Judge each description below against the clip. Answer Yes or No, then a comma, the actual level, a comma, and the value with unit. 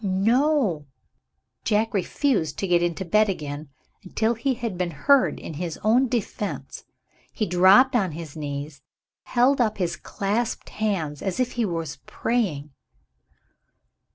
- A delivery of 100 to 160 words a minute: Yes, average, 140 wpm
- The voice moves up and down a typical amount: No, wide, 6.0 semitones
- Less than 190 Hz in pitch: No, high, 195 Hz